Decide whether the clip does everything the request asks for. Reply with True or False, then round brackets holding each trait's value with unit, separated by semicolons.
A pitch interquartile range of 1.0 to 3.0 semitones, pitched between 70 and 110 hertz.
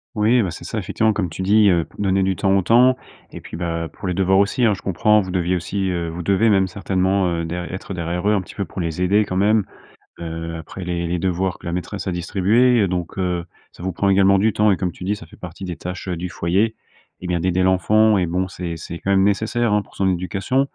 True (2.5 semitones; 95 Hz)